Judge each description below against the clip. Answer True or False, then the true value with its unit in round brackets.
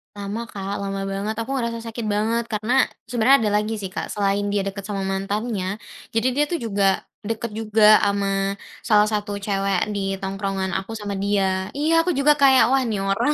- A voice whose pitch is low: False (210 Hz)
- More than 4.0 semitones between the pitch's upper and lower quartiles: False (2.7 semitones)